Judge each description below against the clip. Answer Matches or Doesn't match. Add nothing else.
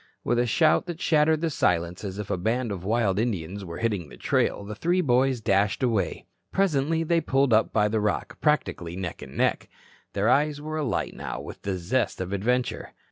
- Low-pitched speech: Matches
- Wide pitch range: Matches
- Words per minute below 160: Doesn't match